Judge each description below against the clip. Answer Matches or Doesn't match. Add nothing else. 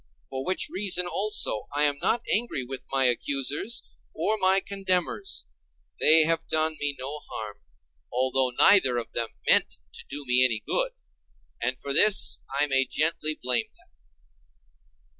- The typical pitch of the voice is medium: Matches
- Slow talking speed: Doesn't match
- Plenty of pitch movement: Matches